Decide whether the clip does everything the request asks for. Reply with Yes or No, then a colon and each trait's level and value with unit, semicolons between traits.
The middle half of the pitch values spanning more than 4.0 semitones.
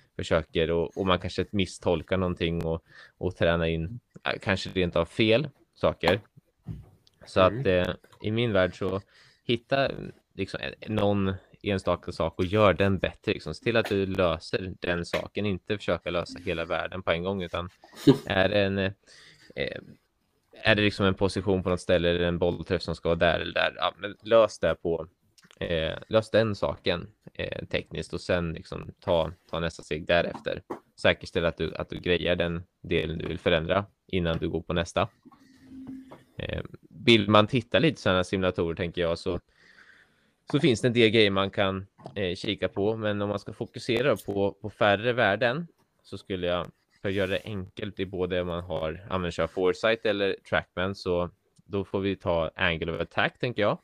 No: average, 3.2 semitones